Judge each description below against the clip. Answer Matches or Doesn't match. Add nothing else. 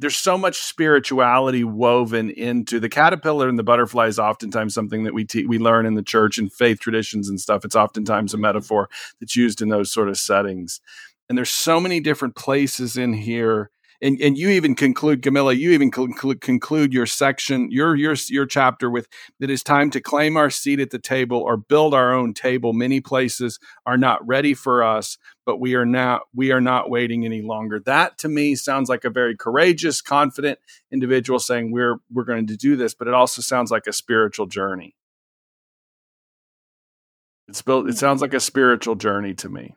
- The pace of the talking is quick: Doesn't match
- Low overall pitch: Matches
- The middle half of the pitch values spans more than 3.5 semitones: Doesn't match